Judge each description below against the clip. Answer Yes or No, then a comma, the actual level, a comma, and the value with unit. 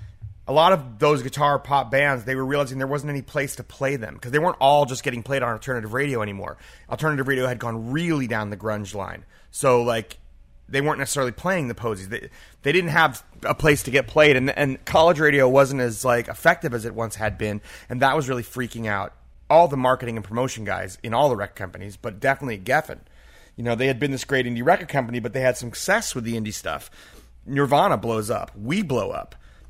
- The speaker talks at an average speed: No, fast, 225 wpm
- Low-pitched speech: Yes, low, 130 Hz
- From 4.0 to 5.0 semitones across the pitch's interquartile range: Yes, average, 4.3 semitones